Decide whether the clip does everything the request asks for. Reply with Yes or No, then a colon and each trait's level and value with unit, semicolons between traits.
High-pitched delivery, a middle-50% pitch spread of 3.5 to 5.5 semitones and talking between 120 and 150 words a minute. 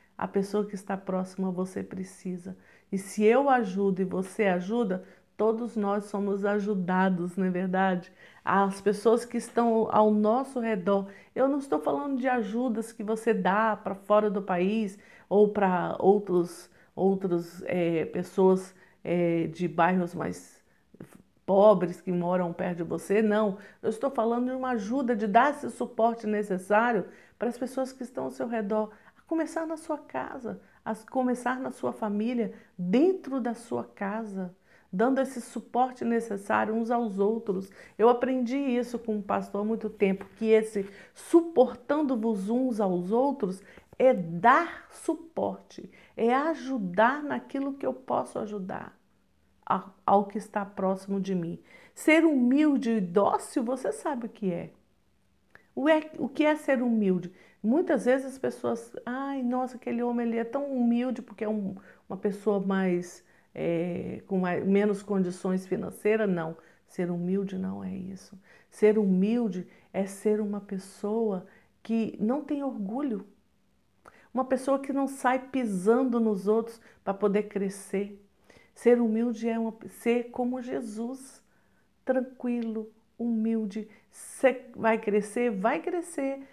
Yes: high, 215 Hz; average, 4.0 semitones; average, 145 wpm